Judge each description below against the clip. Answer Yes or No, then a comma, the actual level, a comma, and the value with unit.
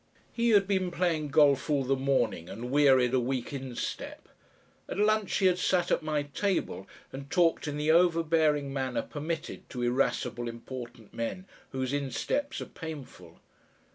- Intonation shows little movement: No, average, 4.7 semitones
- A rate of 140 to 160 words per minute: Yes, average, 155 wpm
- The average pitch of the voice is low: No, medium, 145 Hz